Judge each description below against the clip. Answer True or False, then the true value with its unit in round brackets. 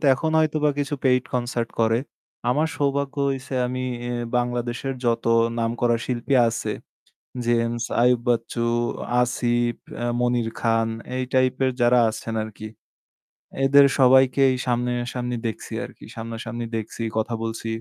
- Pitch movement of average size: False (2.0 semitones)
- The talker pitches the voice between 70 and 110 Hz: False (120 Hz)